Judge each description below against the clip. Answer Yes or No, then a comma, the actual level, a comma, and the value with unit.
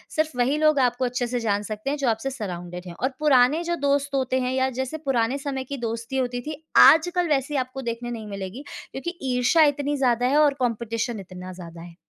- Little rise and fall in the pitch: No, average, 3.7 semitones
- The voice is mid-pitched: No, very high, 255 Hz